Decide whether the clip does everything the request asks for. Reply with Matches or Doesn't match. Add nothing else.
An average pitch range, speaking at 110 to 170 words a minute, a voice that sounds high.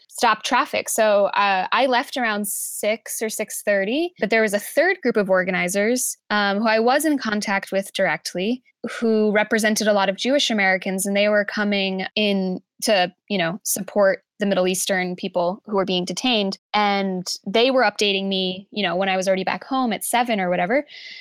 Doesn't match